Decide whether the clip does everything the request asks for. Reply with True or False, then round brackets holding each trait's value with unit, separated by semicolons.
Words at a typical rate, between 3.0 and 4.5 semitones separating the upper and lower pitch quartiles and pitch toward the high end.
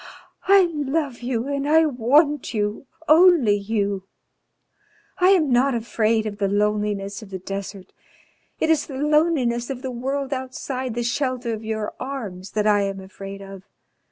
False (155 wpm; 5.2 semitones; 240 Hz)